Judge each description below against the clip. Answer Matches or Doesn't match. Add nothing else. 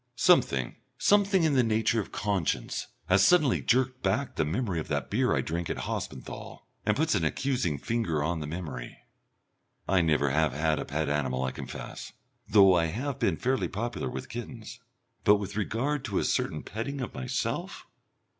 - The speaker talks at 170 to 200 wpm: Matches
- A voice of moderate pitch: Doesn't match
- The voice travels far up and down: Matches